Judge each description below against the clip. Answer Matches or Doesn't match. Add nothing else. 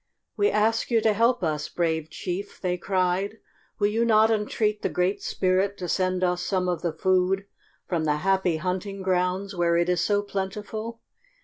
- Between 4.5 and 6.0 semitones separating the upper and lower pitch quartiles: Doesn't match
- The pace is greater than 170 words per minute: Matches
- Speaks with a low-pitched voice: Doesn't match